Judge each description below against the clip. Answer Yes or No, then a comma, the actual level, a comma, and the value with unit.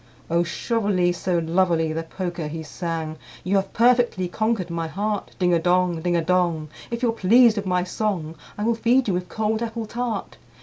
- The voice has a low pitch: No, medium, 185 Hz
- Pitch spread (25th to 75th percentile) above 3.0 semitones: Yes, average, 4.4 semitones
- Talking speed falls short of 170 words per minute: No, average, 200 wpm